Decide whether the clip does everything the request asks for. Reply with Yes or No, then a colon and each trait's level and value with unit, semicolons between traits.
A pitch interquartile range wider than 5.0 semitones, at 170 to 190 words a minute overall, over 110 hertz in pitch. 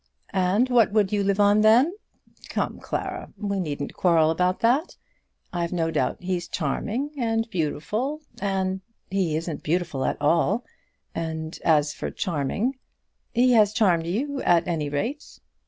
No: wide, 5.5 semitones; average, 155 wpm; high, 190 Hz